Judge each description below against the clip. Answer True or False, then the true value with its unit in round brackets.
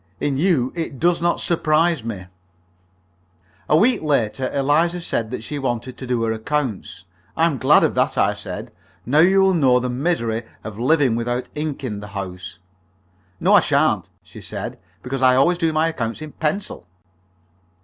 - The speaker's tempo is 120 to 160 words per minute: False (175 wpm)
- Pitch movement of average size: False (5.7 semitones)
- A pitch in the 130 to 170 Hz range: True (135 Hz)